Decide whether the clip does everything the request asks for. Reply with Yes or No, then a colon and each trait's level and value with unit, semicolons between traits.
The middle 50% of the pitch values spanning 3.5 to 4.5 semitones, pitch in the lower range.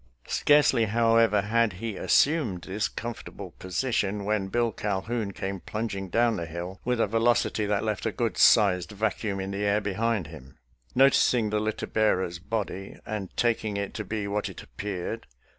No: average, 2.9 semitones; low, 105 Hz